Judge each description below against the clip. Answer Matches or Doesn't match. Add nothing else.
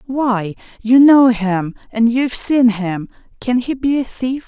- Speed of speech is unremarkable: Matches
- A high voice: Matches